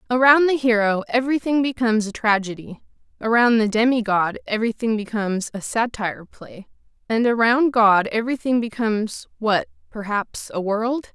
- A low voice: No, high, 225 Hz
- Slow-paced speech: Yes, slow, 125 wpm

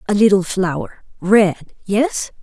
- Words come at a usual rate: No, slow, 75 wpm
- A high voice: Yes, high, 195 Hz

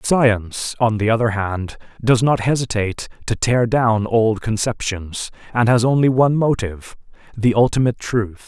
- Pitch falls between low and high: No, low, 115 Hz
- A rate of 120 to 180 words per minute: Yes, average, 150 wpm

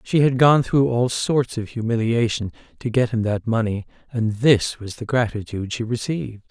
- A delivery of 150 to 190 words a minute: Yes, average, 185 wpm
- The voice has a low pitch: Yes, low, 115 Hz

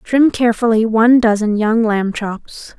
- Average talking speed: Yes, average, 150 wpm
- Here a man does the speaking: No, female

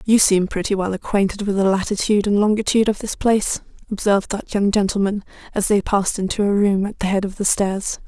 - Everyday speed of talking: No, fast, 215 wpm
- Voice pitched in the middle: No, high, 200 Hz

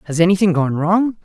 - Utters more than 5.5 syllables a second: Yes, 5.8 syllables/s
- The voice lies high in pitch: No, medium, 180 Hz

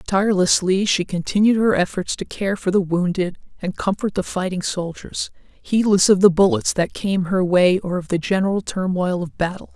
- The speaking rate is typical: Yes, average, 185 wpm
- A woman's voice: Yes, female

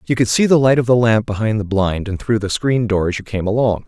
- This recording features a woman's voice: No, male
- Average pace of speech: No, fast, 310 wpm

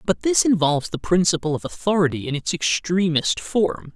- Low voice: No, medium, 175 Hz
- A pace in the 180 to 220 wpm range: No, average, 165 wpm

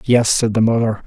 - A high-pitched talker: No, low, 110 Hz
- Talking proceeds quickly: Yes, fast, 225 wpm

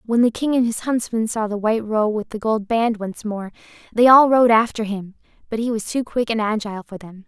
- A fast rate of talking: Yes, fast, 245 wpm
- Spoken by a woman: Yes, female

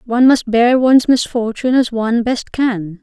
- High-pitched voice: Yes, high, 235 Hz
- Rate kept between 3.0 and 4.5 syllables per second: No, 5.2 syllables/s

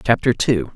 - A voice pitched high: No, low, 110 Hz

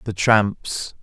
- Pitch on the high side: No, low, 105 Hz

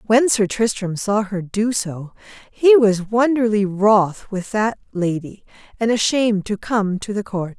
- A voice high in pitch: Yes, high, 210 Hz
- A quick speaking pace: No, average, 165 wpm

